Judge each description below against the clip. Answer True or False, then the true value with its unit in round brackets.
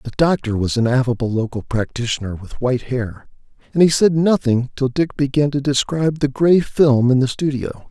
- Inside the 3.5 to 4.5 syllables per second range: False (5.2 syllables/s)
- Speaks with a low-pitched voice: True (130 Hz)